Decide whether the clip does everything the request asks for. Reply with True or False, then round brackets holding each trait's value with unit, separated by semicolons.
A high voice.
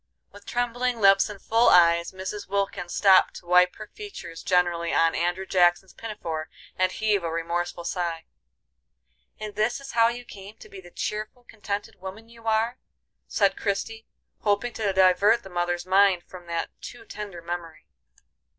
True (195 Hz)